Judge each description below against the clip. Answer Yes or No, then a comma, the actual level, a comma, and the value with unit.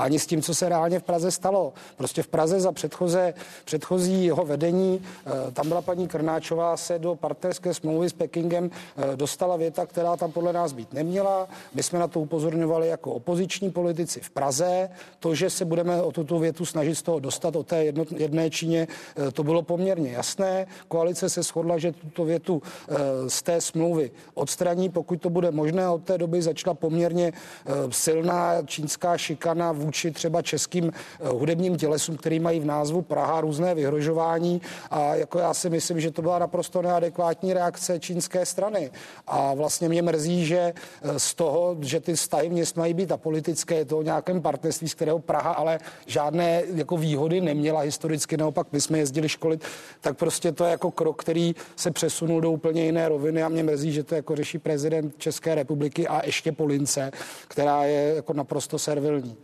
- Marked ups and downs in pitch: No, narrow, 2.1 semitones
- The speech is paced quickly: Yes, fast, 180 wpm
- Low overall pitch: No, medium, 165 Hz